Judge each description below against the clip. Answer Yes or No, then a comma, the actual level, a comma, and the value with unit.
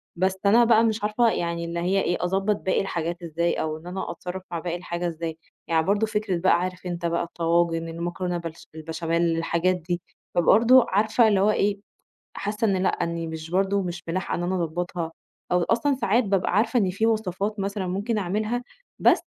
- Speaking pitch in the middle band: Yes, medium, 180 Hz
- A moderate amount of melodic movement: Yes, average, 3.3 semitones